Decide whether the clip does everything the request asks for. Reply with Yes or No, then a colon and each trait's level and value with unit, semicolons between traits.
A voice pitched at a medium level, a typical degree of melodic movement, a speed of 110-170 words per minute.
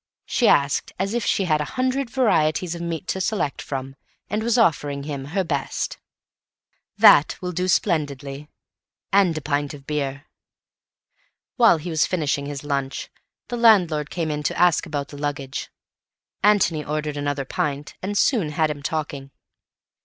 Yes: medium, 155 Hz; average, 4.4 semitones; average, 160 wpm